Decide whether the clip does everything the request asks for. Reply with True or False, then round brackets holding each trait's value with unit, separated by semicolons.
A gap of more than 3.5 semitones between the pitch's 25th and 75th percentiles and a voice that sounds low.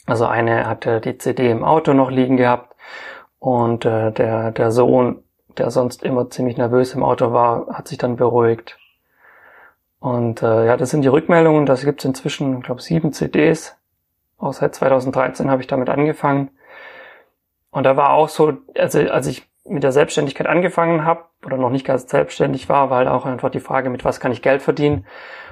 False (2.9 semitones; 130 Hz)